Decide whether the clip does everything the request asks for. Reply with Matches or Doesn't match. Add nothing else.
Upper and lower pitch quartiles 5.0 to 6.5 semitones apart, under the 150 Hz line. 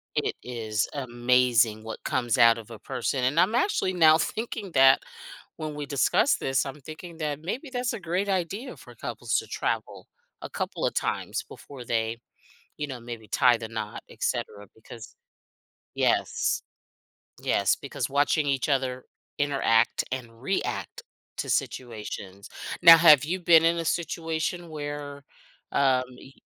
Matches